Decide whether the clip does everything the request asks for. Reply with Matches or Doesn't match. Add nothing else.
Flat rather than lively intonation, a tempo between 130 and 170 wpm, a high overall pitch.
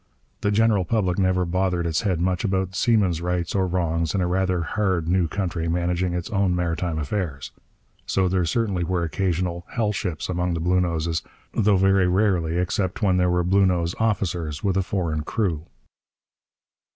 Doesn't match